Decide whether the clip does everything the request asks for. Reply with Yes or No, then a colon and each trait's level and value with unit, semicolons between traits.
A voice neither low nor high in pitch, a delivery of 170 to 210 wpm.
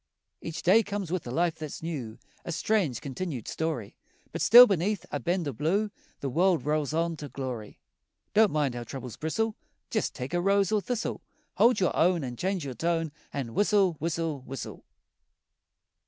Yes: medium, 165 Hz; average, 175 wpm